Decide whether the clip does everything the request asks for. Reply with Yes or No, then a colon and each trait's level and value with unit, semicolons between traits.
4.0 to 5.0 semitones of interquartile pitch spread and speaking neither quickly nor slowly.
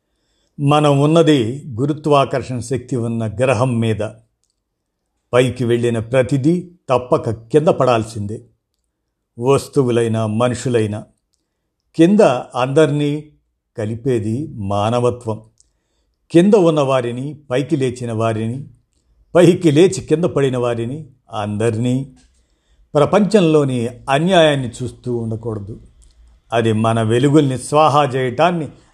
Yes: average, 4.5 semitones; average, 80 wpm